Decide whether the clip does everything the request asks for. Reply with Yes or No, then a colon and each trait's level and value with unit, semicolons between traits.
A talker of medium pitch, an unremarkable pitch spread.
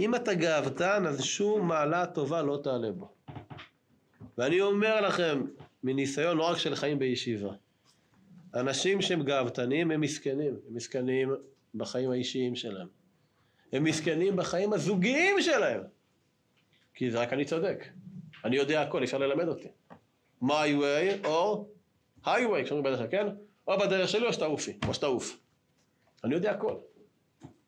No: medium, 155 Hz; wide, 6.6 semitones